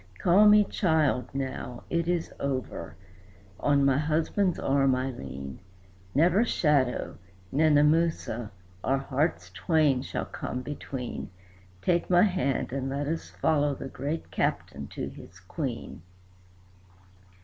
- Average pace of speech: No, slow, 120 wpm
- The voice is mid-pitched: Yes, medium, 145 Hz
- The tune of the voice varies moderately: Yes, average, 3.7 semitones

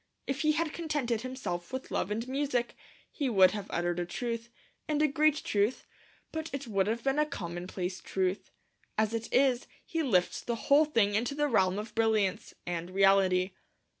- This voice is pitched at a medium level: No, high, 230 Hz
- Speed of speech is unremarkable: Yes, average, 180 wpm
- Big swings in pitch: Yes, wide, 6.4 semitones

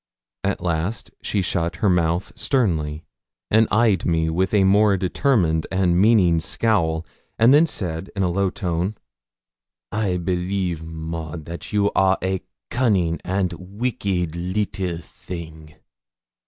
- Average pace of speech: No, slow, 130 wpm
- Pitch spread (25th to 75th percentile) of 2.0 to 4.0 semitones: Yes, average, 3.4 semitones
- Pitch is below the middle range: Yes, very low, 90 Hz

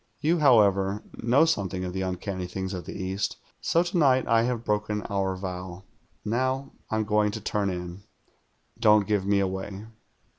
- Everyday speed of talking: Yes, average, 170 wpm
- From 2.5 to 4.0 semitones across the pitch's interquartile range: Yes, average, 3.5 semitones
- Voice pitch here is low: Yes, low, 100 Hz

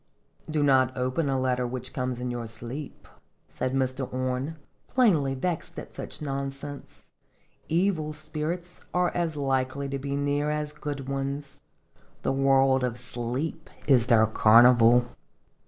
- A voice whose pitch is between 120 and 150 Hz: Yes, low, 135 Hz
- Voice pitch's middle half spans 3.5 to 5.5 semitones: No, average, 2.9 semitones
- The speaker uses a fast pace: No, average, 145 wpm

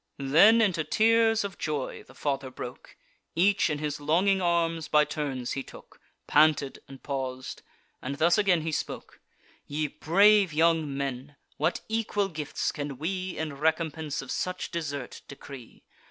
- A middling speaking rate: Yes, average, 150 wpm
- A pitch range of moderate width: Yes, average, 4.4 semitones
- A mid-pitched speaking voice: Yes, medium, 155 Hz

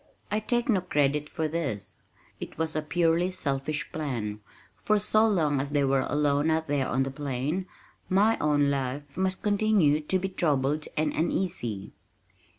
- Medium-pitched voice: Yes, medium, 150 Hz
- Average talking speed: Yes, average, 160 wpm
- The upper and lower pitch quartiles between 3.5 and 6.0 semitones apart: Yes, average, 4.7 semitones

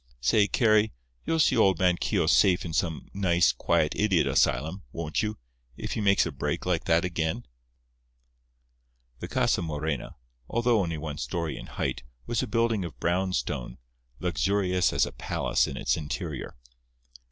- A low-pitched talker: Yes, very low, 85 Hz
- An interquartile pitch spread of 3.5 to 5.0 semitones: Yes, average, 4.3 semitones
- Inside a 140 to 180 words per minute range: Yes, average, 155 wpm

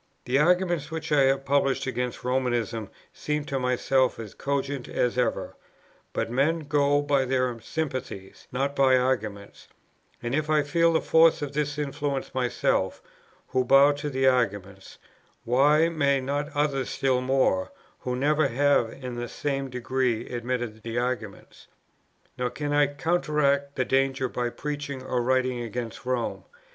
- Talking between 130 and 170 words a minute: Yes, average, 150 wpm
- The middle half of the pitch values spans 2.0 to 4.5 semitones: Yes, narrow, 2.6 semitones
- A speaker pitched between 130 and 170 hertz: Yes, low, 135 Hz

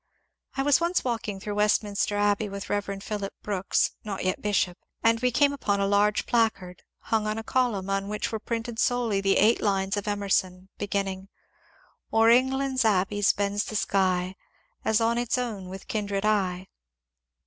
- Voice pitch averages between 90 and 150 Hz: No, high, 205 Hz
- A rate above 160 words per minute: Yes, average, 170 wpm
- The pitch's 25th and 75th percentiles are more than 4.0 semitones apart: No, narrow, 2.5 semitones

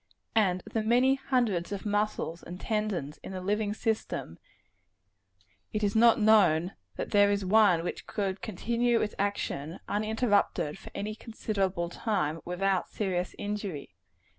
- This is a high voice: Yes, high, 205 Hz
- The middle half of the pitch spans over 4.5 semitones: No, average, 3.2 semitones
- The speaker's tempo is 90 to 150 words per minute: Yes, average, 140 wpm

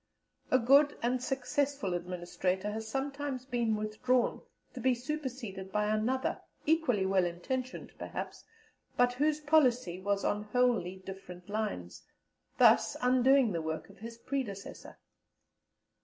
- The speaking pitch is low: No, high, 235 Hz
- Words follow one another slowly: Yes, slow, 125 wpm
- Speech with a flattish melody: No, average, 5.2 semitones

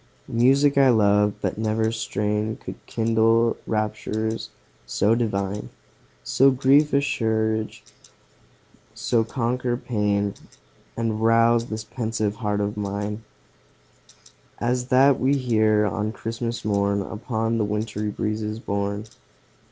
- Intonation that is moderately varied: No, narrow, 2.0 semitones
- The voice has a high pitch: No, low, 110 Hz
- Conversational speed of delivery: No, slow, 110 wpm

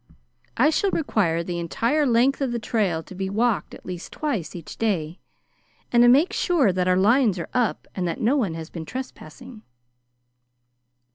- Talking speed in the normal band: Yes, average, 170 wpm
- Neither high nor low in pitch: No, high, 220 Hz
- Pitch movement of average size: No, wide, 6.4 semitones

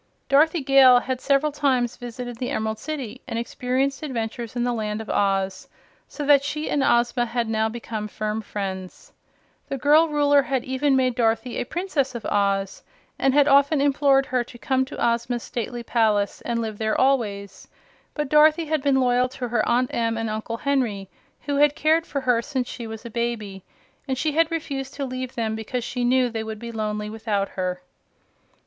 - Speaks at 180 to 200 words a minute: Yes, average, 190 wpm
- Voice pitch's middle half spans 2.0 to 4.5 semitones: Yes, average, 3.8 semitones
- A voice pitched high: Yes, high, 245 Hz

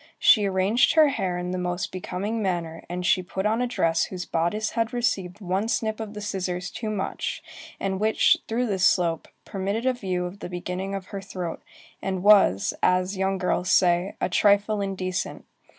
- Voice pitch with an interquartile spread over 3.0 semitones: No, average, 2.7 semitones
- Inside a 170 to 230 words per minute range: Yes, average, 185 wpm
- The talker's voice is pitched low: No, high, 190 Hz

